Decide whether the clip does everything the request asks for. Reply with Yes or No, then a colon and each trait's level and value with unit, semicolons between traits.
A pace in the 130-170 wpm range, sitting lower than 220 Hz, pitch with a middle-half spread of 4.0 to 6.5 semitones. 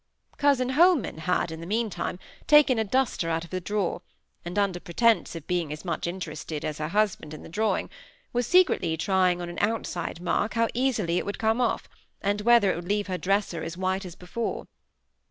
No: average, 200 wpm; high, 190 Hz; average, 4.8 semitones